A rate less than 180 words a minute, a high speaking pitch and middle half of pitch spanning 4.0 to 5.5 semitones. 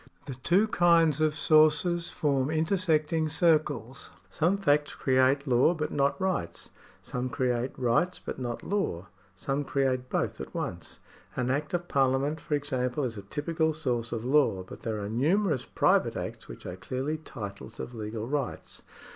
No: average, 160 wpm; medium, 140 Hz; average, 4.3 semitones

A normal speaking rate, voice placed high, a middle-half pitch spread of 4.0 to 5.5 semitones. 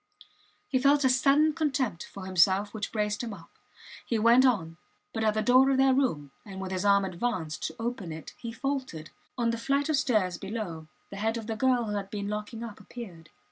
No: fast, 215 wpm; high, 220 Hz; average, 4.9 semitones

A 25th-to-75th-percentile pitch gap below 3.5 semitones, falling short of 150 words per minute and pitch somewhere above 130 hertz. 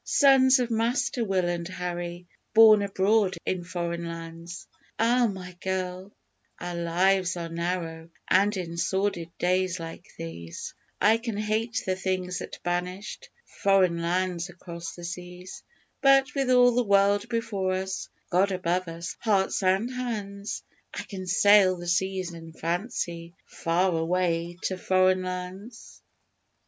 Yes: average, 2.8 semitones; slow, 135 wpm; medium, 185 Hz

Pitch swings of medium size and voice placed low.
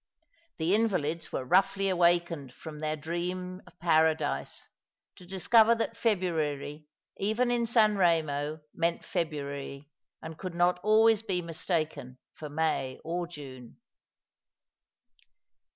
No: average, 3.9 semitones; medium, 170 Hz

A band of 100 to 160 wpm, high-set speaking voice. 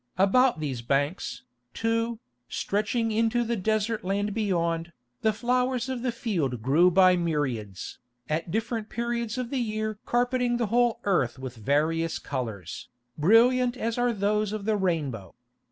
Yes: average, 145 wpm; high, 210 Hz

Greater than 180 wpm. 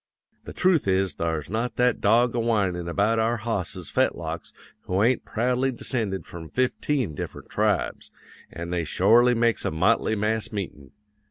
No: average, 155 wpm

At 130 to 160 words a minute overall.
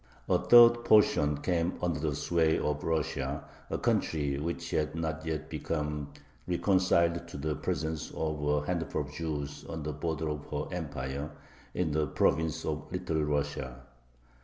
Yes: average, 155 wpm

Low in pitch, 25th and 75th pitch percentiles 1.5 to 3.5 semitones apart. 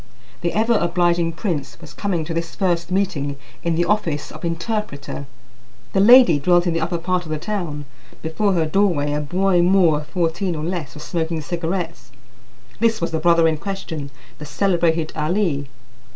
No: medium, 170 Hz; average, 3.1 semitones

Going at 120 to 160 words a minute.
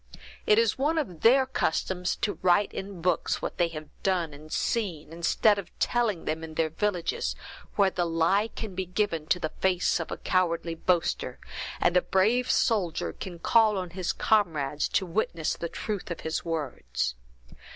No: average, 180 wpm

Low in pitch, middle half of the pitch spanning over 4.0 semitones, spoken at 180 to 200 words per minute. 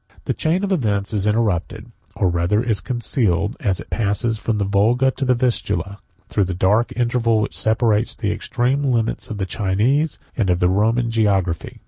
No: low, 110 Hz; average, 3.4 semitones; average, 185 wpm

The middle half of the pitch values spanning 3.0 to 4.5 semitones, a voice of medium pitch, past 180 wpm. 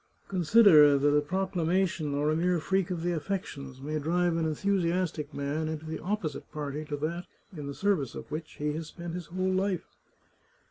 Yes: average, 3.4 semitones; medium, 160 Hz; average, 190 wpm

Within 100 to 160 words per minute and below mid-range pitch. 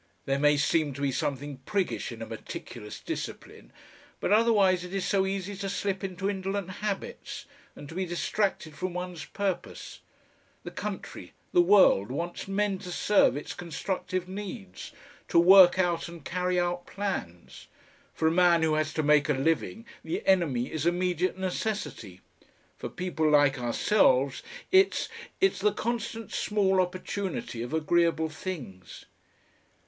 No: average, 150 wpm; medium, 180 Hz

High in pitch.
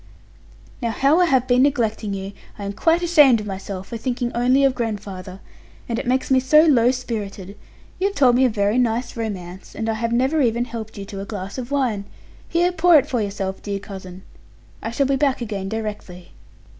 Yes: high, 230 Hz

